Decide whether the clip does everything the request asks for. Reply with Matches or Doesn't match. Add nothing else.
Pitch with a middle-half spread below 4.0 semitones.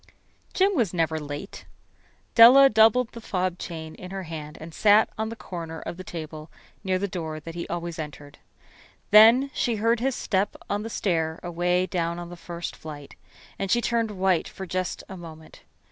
Doesn't match